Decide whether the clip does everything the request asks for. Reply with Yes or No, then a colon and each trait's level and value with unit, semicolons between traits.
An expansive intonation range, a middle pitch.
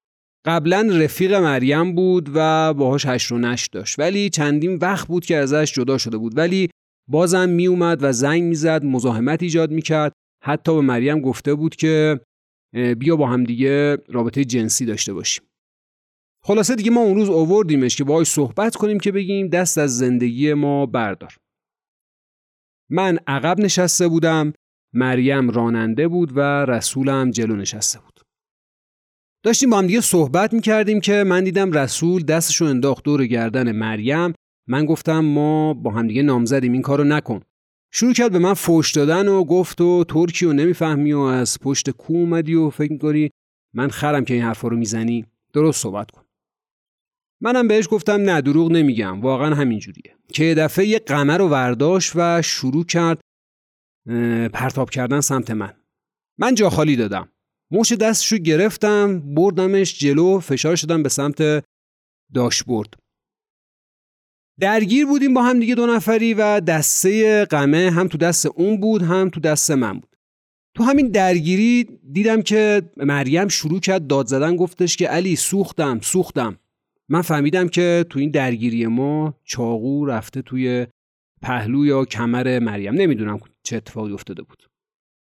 Yes: wide, 5.8 semitones; medium, 150 Hz